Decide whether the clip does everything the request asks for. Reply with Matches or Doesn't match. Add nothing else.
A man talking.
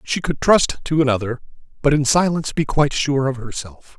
Matches